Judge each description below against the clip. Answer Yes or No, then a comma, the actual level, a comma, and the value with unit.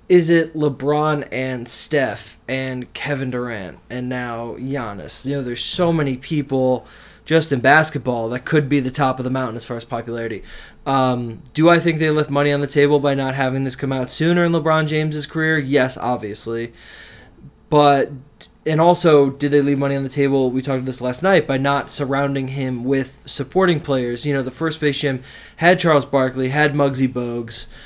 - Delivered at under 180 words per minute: No, average, 195 wpm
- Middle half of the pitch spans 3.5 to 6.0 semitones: No, average, 2.9 semitones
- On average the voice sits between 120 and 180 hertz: Yes, low, 135 Hz